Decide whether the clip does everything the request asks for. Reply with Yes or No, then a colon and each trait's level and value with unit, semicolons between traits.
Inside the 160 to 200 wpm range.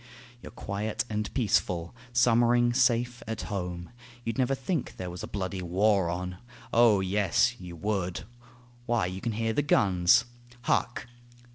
No: average, 145 wpm